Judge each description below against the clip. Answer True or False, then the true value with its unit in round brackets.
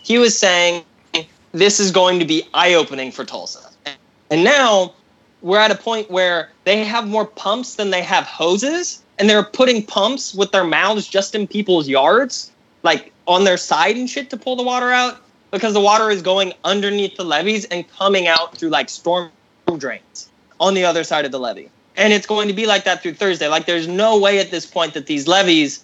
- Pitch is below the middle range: False (195 Hz)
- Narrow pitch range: False (3.6 semitones)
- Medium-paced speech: False (210 wpm)